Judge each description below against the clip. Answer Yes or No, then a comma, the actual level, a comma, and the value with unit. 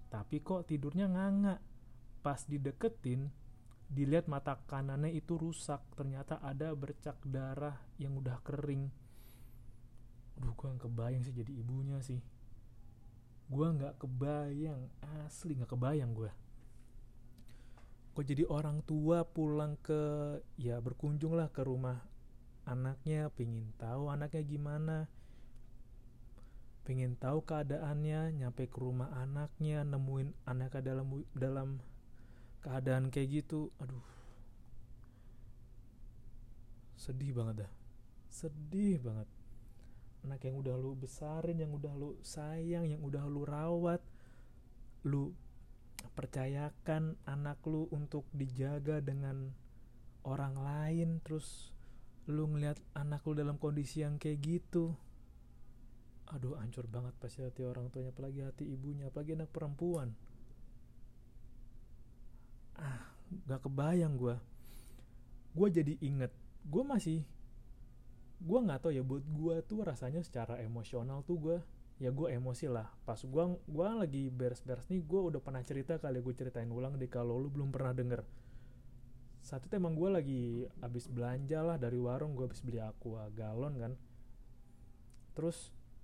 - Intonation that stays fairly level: No, average, 4.0 semitones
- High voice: No, low, 135 Hz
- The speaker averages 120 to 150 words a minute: Yes, average, 125 wpm